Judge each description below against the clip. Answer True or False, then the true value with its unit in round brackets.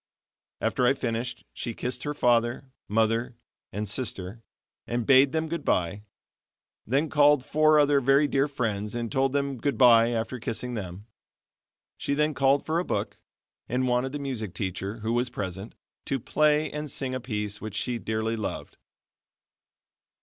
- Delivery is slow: False (155 wpm)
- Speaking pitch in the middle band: False (125 Hz)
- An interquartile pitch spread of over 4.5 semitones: False (4.0 semitones)